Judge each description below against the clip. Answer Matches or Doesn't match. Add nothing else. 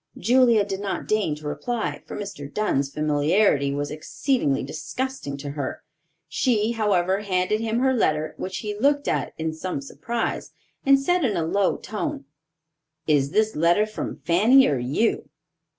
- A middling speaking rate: Matches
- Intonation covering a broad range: Matches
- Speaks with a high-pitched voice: Matches